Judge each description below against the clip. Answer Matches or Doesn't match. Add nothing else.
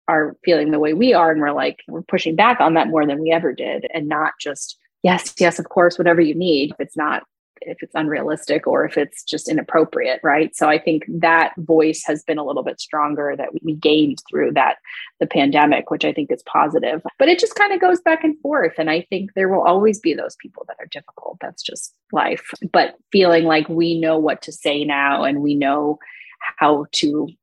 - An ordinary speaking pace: Doesn't match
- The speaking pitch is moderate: Matches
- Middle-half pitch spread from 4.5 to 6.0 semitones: Matches